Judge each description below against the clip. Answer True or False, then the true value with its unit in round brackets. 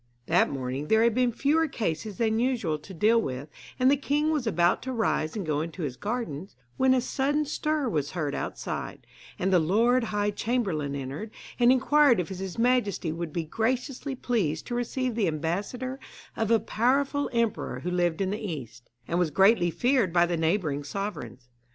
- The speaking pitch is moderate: False (205 Hz)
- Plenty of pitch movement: True (7.4 semitones)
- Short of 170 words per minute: False (185 wpm)